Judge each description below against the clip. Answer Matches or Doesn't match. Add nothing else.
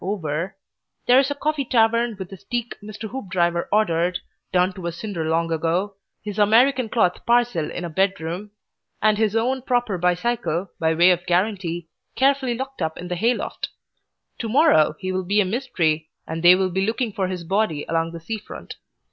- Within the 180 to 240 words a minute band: Matches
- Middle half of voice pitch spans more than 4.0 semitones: Matches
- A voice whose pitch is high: Matches